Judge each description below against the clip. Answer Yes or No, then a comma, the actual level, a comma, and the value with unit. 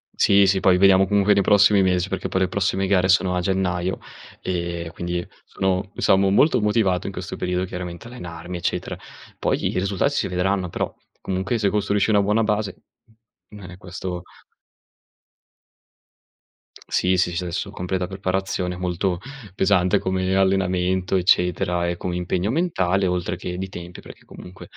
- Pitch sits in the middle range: No, very low, 95 Hz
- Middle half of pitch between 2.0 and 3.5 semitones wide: No, narrow, 1.6 semitones